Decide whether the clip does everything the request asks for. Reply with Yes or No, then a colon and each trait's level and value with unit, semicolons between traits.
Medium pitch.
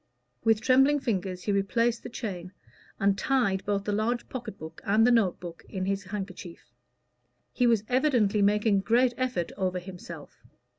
No: high, 205 Hz